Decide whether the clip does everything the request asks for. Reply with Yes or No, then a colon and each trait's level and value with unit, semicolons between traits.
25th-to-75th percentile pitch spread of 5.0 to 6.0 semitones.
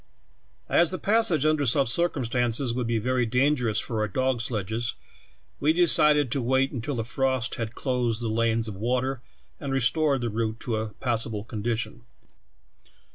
No: average, 3.0 semitones